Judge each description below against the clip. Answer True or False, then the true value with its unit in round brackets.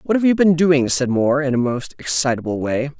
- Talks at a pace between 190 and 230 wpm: False (240 wpm)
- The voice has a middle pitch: True (145 Hz)